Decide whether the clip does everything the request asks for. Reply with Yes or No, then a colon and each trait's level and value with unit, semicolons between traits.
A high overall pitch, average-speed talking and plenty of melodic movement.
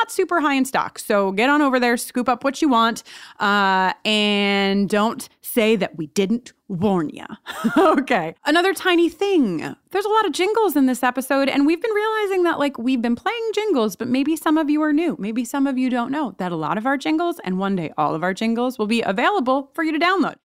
No: very high, 260 Hz; fast, 230 wpm; wide, 7.2 semitones